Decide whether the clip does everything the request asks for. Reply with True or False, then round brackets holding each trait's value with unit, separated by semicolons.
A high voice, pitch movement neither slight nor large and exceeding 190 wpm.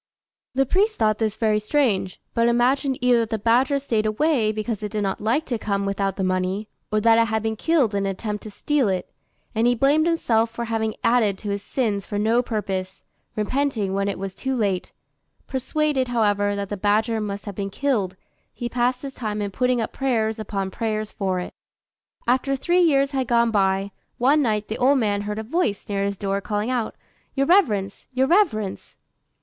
True (220 Hz; 3.8 semitones; 200 wpm)